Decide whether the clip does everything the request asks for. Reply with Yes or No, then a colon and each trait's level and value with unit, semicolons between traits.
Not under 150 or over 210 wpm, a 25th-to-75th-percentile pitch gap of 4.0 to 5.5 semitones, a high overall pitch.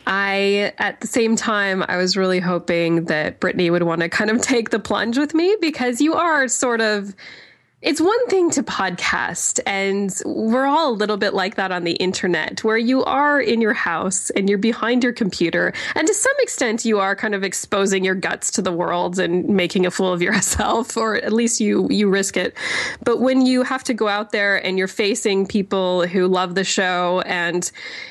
Yes: fast, 205 wpm; average, 4.5 semitones; high, 205 Hz